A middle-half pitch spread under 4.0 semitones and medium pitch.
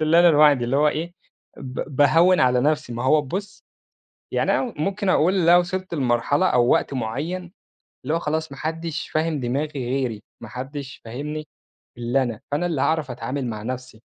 No: average, 4.3 semitones; medium, 145 Hz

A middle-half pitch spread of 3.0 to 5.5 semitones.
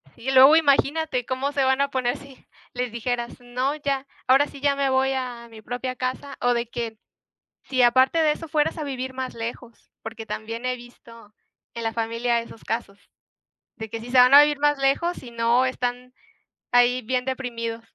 No: narrow, 2.5 semitones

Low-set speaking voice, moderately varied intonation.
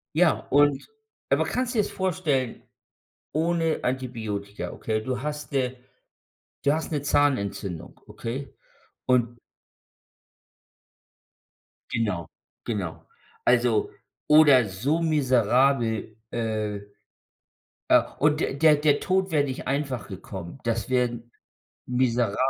Yes: low, 130 Hz; average, 4.8 semitones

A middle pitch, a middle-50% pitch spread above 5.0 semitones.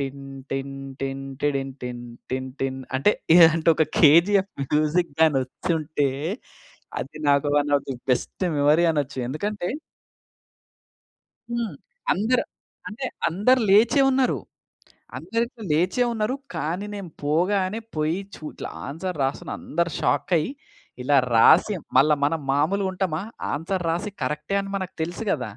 Yes: medium, 160 Hz; wide, 5.5 semitones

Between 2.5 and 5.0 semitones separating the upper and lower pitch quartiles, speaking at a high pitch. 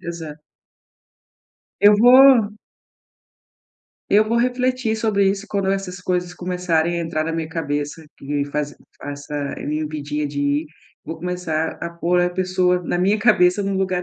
No: average, 3.9 semitones; medium, 180 Hz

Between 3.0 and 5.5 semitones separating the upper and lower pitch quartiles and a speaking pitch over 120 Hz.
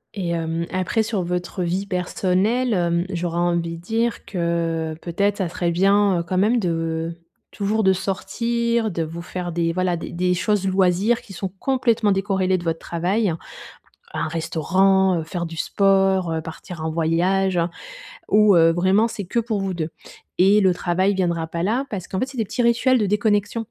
Yes: average, 3.3 semitones; medium, 185 Hz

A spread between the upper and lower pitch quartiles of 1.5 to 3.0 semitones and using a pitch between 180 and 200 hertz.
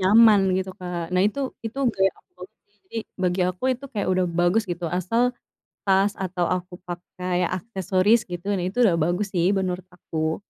Yes: narrow, 2.5 semitones; medium, 185 Hz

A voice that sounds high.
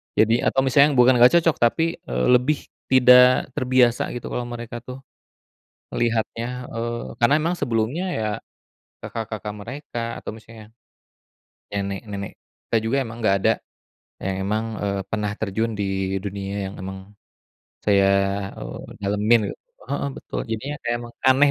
No: low, 115 Hz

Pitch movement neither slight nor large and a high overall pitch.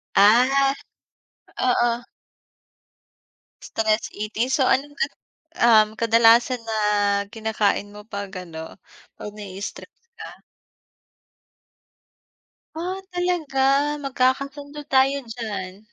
Yes: average, 4.3 semitones; high, 230 Hz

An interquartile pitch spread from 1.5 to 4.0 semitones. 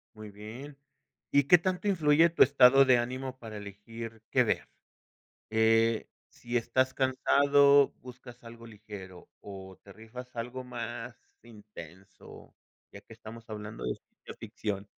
Yes: average, 3.5 semitones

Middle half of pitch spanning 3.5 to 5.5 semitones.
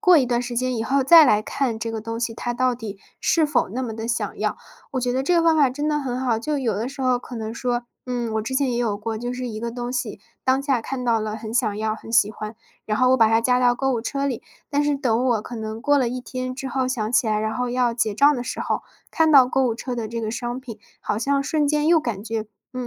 No: average, 2.8 semitones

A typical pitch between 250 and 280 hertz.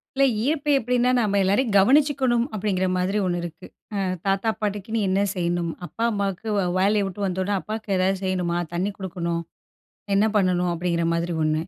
No: high, 195 Hz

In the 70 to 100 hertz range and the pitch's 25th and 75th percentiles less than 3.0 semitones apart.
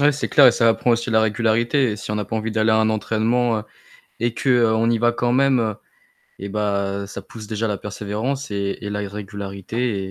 No: low, 110 Hz; narrow, 2.4 semitones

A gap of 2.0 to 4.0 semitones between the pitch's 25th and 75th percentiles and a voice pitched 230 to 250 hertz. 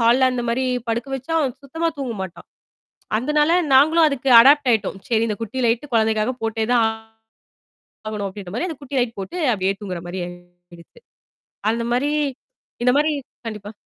No: average, 4.4 semitones; high, 235 Hz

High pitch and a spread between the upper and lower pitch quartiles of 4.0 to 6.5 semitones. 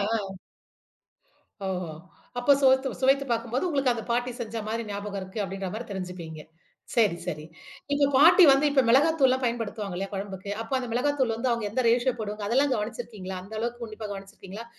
Yes: high, 230 Hz; average, 4.7 semitones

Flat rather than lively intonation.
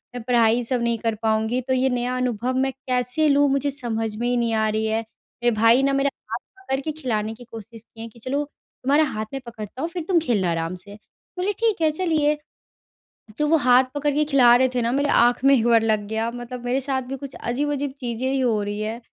No: average, 3.3 semitones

